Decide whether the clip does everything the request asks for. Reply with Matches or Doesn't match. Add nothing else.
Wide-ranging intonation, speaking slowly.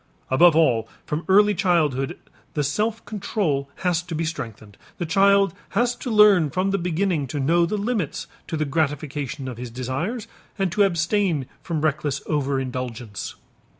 Doesn't match